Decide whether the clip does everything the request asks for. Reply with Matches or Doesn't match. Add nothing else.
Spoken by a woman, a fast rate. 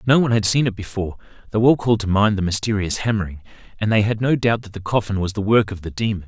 Doesn't match